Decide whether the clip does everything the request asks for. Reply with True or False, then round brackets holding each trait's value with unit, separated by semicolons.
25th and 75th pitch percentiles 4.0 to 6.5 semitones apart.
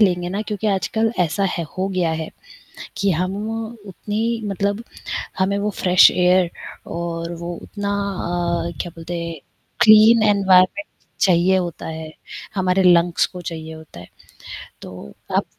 False (2.7 semitones)